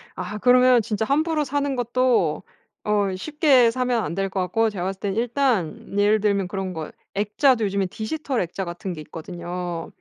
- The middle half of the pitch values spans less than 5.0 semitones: No, average, 5.3 semitones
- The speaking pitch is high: Yes, high, 210 Hz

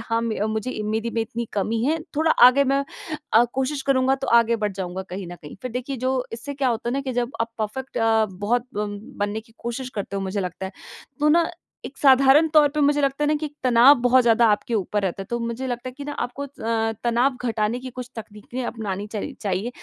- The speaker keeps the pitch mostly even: No, average, 3.5 semitones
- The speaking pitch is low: No, high, 235 Hz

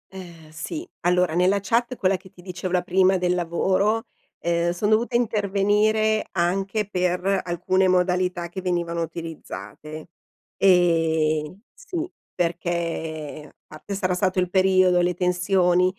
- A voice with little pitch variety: Yes, narrow, 2.1 semitones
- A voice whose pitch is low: No, medium, 180 Hz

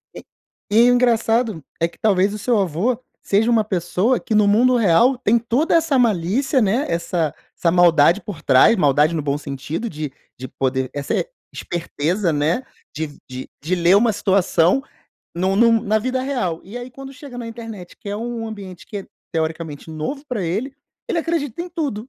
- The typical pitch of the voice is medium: No, high, 205 Hz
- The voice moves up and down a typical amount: No, wide, 6.4 semitones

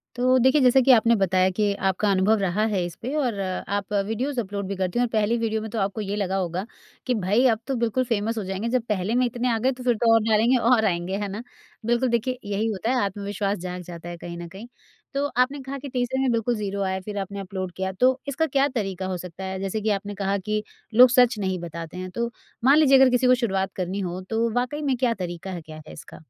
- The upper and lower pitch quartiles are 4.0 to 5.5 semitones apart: Yes, average, 4.4 semitones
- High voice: Yes, high, 215 Hz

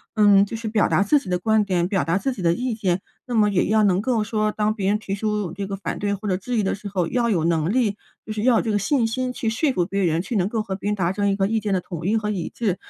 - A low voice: No, high, 205 Hz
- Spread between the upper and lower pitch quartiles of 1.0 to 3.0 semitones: Yes, narrow, 2.5 semitones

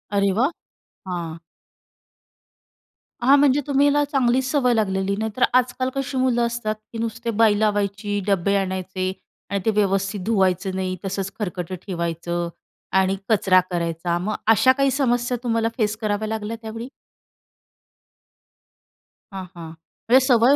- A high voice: Yes, high, 210 Hz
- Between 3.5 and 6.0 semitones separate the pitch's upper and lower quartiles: Yes, average, 4.1 semitones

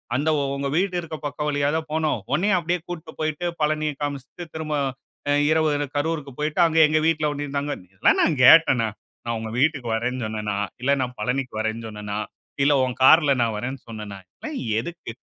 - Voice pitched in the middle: Yes, medium, 145 Hz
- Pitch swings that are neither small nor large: Yes, average, 4.4 semitones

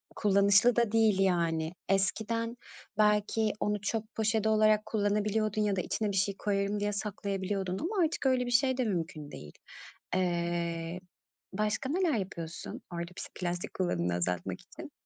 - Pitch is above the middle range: Yes, high, 205 Hz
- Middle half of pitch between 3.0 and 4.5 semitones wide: Yes, average, 3.4 semitones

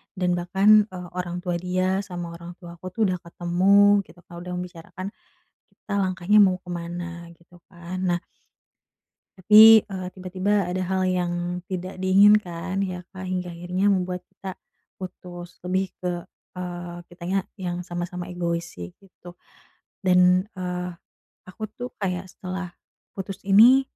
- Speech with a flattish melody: Yes, narrow, 1.4 semitones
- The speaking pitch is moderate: Yes, medium, 180 Hz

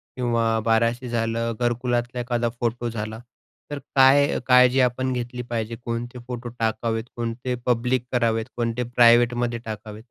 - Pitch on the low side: Yes, low, 120 Hz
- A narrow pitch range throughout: Yes, narrow, 1.2 semitones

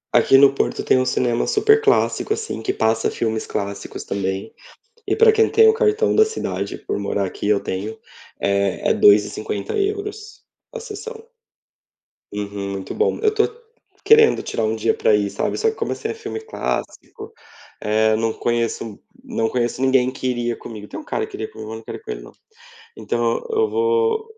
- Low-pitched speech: Yes, low, 125 Hz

